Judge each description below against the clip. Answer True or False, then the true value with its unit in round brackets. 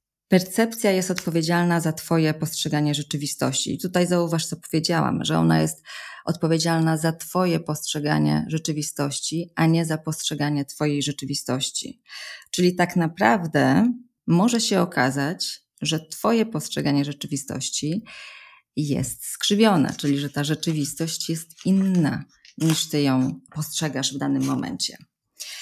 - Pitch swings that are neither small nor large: True (3.6 semitones)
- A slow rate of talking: False (120 wpm)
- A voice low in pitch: False (160 Hz)